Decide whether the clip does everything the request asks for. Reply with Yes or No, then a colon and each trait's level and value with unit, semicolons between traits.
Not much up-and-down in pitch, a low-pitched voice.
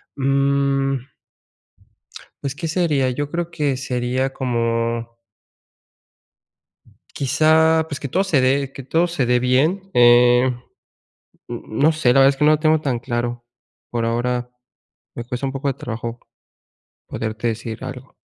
No: average, 3.2 semitones; low, 130 Hz